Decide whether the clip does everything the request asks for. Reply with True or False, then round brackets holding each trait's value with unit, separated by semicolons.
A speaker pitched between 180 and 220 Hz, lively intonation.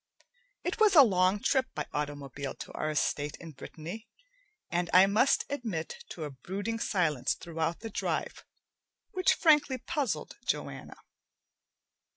True (185 Hz; 8.2 semitones)